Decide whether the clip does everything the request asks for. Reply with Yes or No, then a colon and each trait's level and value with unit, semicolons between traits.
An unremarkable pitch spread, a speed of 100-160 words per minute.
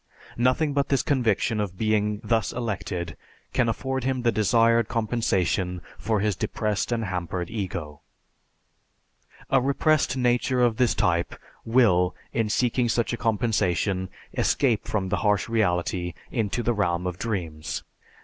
Yes: average, 4.6 semitones; average, 140 wpm